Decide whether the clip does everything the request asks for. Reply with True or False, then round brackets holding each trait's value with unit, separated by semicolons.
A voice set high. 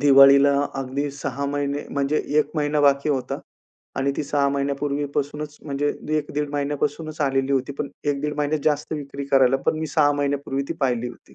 False (140 Hz)